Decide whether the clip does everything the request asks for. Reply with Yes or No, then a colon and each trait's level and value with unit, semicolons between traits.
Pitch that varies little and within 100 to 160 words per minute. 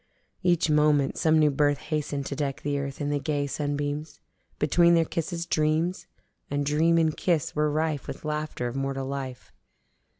No: narrow, 1.9 semitones; average, 170 wpm